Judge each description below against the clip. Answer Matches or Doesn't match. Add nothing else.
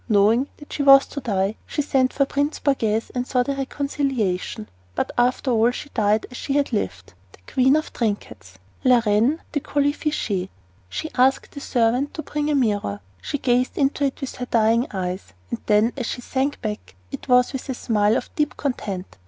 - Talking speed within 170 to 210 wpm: Matches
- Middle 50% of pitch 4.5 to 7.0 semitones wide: Matches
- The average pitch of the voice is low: Doesn't match